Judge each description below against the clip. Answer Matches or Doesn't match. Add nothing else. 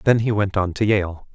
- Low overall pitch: Matches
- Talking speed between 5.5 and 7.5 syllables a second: Doesn't match